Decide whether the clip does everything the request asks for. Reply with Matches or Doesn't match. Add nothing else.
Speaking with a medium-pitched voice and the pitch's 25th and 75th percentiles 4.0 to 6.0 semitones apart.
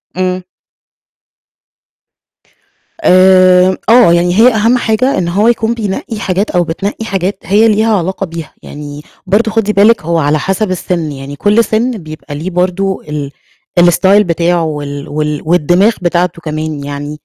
Matches